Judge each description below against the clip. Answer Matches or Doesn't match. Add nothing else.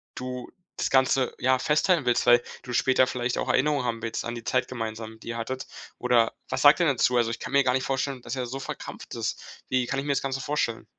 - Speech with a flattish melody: Matches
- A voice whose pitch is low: Matches